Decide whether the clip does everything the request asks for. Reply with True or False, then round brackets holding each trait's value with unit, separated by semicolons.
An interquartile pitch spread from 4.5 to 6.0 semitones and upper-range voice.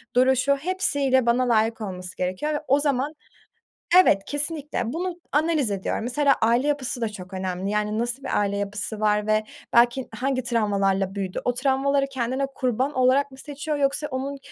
True (4.8 semitones; 255 Hz)